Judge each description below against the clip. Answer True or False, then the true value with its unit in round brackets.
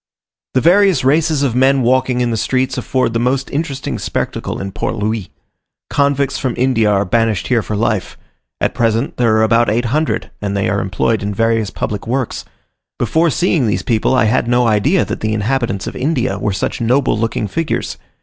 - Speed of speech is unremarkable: True (190 wpm)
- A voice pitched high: False (120 Hz)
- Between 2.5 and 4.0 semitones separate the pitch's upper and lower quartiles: True (3.6 semitones)